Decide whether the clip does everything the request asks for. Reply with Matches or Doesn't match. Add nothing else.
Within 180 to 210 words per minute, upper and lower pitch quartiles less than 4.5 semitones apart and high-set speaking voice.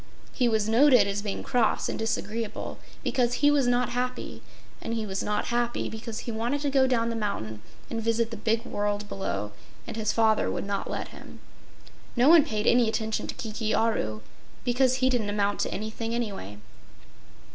Matches